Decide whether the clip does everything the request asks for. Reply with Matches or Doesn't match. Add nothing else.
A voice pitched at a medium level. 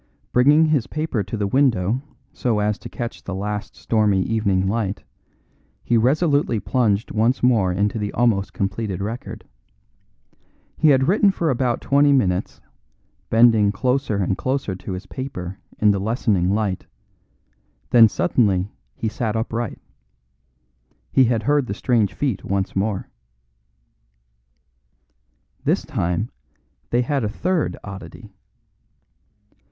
Doesn't match